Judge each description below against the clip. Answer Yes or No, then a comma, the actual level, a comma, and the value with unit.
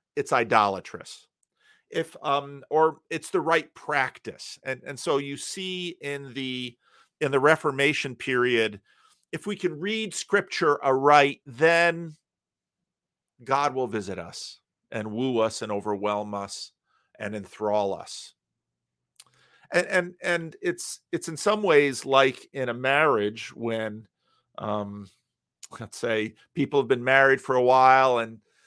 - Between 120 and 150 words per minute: Yes, slow, 135 wpm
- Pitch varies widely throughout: Yes, wide, 6.4 semitones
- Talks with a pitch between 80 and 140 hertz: Yes, low, 135 Hz